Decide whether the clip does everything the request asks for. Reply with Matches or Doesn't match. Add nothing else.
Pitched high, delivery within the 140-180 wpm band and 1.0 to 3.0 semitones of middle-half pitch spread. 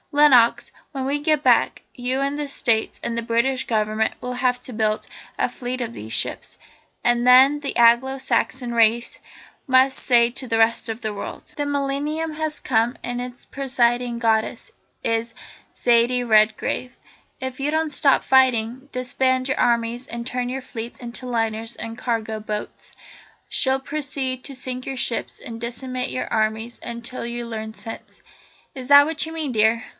Matches